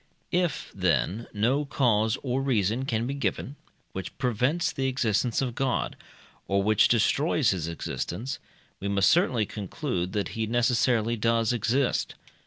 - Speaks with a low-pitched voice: Yes, low, 115 Hz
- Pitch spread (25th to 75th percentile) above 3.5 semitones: Yes, average, 3.9 semitones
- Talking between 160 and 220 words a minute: No, average, 140 wpm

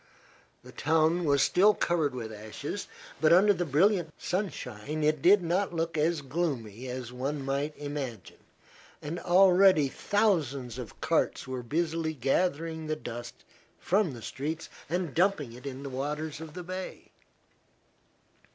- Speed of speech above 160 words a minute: No, average, 140 wpm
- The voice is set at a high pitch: No, medium, 155 Hz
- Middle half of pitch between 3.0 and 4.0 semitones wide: No, average, 4.6 semitones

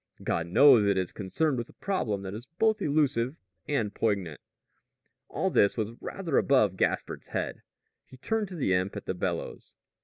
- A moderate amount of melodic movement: No, wide, 6.9 semitones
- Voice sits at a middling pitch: No, low, 115 Hz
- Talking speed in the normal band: Yes, average, 175 wpm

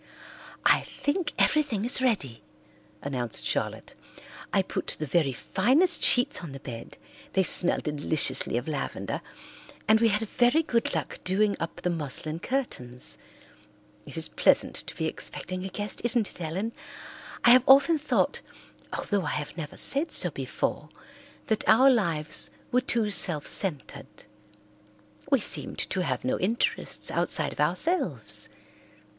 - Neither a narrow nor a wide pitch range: No, wide, 8.4 semitones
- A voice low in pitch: No, high, 190 Hz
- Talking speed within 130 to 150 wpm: Yes, average, 145 wpm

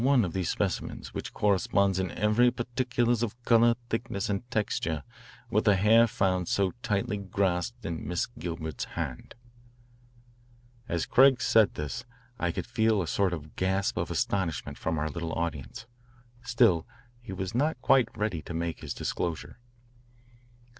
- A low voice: Yes, low, 100 Hz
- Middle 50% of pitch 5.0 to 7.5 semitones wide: Yes, wide, 5.5 semitones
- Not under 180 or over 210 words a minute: No, average, 160 wpm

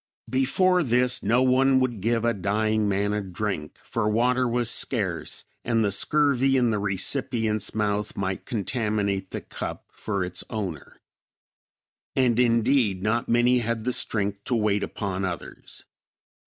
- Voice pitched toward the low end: Yes, low, 110 Hz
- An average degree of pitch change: Yes, average, 3.5 semitones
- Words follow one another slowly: No, average, 145 wpm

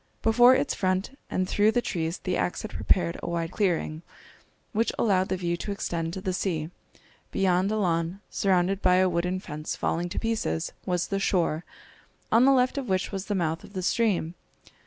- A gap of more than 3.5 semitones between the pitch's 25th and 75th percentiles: No, average, 3.2 semitones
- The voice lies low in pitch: No, medium, 185 Hz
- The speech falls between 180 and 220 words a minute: Yes, average, 195 wpm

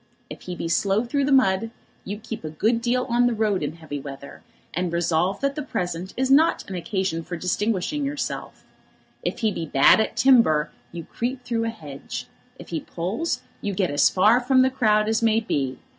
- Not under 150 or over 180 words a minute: No, fast, 205 wpm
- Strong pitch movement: Yes, wide, 6.2 semitones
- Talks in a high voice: Yes, high, 210 Hz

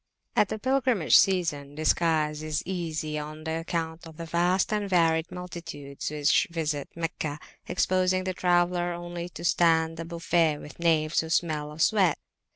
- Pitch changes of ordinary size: No, narrow, 2.2 semitones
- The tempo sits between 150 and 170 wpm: Yes, average, 155 wpm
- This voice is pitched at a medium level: Yes, medium, 165 Hz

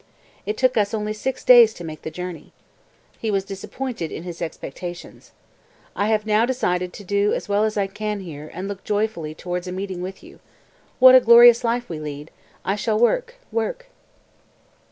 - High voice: Yes, high, 205 Hz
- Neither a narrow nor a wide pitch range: Yes, average, 4.1 semitones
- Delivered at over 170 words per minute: Yes, average, 190 wpm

